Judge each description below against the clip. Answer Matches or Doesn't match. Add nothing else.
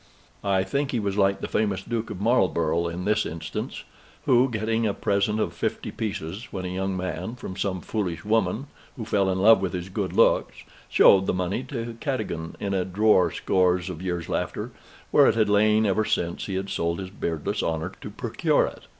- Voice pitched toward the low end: Matches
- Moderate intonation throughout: Matches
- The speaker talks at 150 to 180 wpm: Doesn't match